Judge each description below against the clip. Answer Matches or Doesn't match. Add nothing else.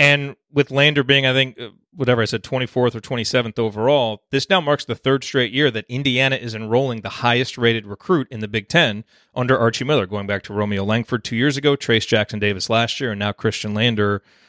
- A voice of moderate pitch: Doesn't match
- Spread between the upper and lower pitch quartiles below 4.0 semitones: Matches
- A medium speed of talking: Doesn't match